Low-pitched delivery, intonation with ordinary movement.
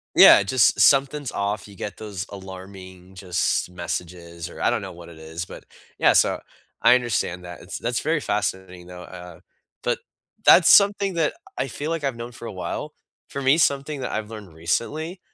No: low, 100 Hz; wide, 7.2 semitones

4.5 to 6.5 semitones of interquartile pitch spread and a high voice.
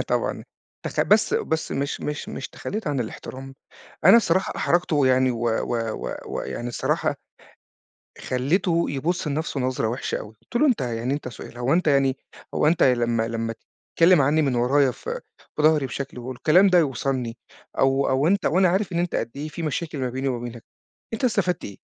No: average, 5.2 semitones; medium, 140 Hz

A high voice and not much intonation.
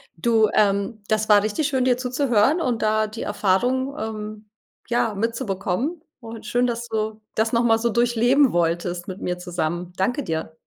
No: high, 220 Hz; average, 3.5 semitones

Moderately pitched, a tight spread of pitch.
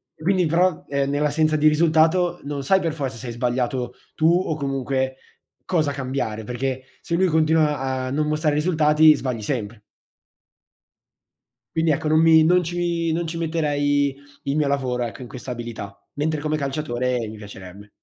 No: medium, 145 Hz; average, 3.7 semitones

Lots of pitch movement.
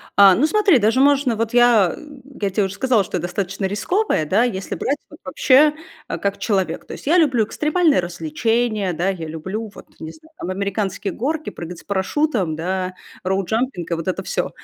Yes: wide, 5.8 semitones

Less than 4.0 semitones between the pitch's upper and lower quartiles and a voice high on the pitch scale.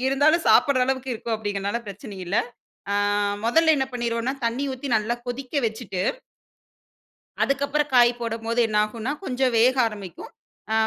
Yes: average, 3.4 semitones; high, 240 Hz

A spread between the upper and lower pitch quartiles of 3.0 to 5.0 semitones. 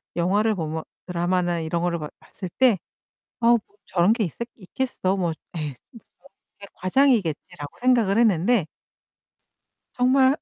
No: wide, 5.5 semitones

